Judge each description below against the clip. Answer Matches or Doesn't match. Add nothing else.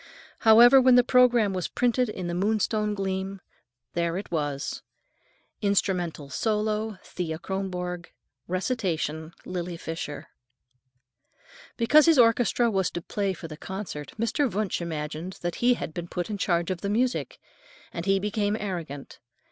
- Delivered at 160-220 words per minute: Doesn't match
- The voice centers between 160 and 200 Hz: Matches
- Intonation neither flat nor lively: Matches